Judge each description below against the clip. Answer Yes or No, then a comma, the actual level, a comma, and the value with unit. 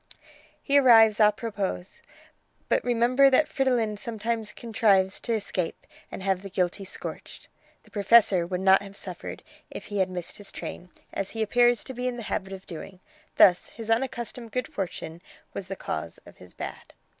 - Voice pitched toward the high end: Yes, high, 210 Hz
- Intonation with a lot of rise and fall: No, average, 3.7 semitones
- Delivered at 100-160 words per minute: No, average, 175 wpm